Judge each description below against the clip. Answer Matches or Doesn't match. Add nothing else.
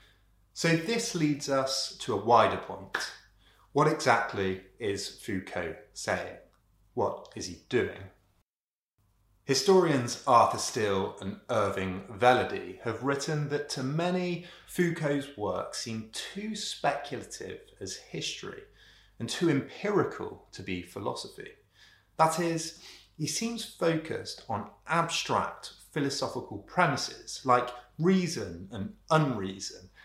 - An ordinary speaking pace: Doesn't match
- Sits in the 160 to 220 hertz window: Doesn't match